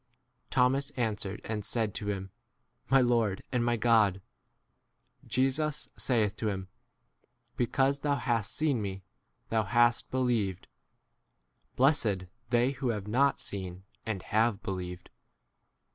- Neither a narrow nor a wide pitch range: Yes, average, 4.1 semitones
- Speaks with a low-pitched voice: Yes, low, 115 Hz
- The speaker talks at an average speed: No, slow, 130 wpm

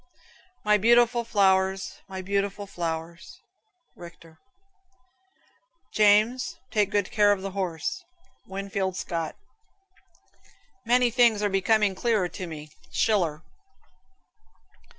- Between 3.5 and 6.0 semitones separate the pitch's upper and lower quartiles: No, average, 3.0 semitones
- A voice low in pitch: No, high, 195 Hz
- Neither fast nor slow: No, slow, 95 wpm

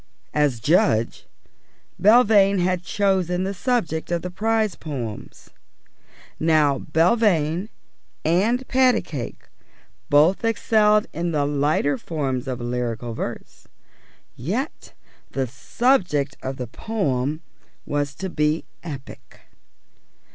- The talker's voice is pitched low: No, medium, 160 Hz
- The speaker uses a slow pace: Yes, slow, 100 wpm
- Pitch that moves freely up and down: Yes, wide, 6.3 semitones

